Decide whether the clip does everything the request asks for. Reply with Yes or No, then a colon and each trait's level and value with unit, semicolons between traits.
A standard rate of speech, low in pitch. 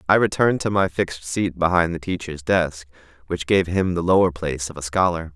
No: fast, 215 wpm; very low, 85 Hz